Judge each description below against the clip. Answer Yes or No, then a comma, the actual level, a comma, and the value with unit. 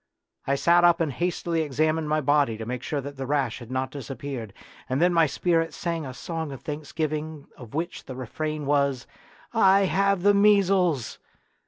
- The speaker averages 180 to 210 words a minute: Yes, average, 185 wpm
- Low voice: No, medium, 155 Hz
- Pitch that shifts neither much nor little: Yes, average, 3.9 semitones